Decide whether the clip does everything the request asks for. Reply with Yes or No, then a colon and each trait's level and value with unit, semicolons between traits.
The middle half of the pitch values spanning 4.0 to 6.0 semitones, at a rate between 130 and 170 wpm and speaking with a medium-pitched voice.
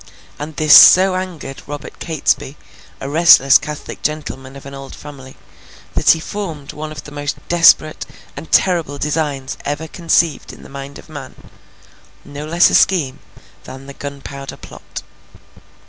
No: narrow, 2.6 semitones; average, 150 wpm; medium, 145 Hz